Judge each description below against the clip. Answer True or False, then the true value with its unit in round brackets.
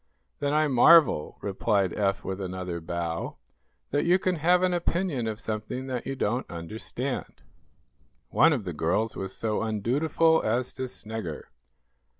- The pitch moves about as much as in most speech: False (7.1 semitones)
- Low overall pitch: True (115 Hz)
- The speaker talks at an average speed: True (150 wpm)